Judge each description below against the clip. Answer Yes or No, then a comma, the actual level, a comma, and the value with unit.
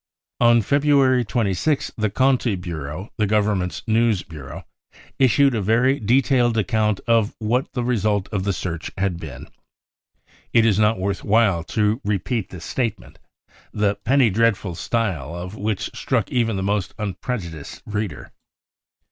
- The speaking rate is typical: Yes, average, 145 wpm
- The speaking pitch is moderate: No, low, 105 Hz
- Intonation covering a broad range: No, average, 3.8 semitones